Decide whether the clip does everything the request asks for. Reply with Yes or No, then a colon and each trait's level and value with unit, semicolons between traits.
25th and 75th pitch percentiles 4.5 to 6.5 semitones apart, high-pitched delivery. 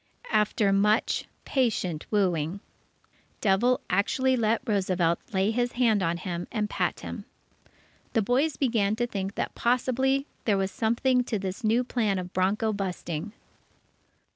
No: average, 4.0 semitones; high, 210 Hz